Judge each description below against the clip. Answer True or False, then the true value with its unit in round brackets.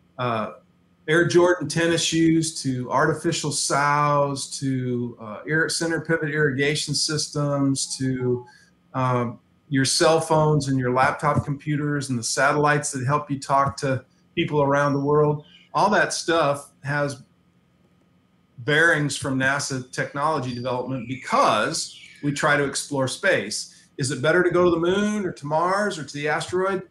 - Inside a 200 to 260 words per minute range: False (145 wpm)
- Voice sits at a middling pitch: True (145 Hz)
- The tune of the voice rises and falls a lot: False (3.0 semitones)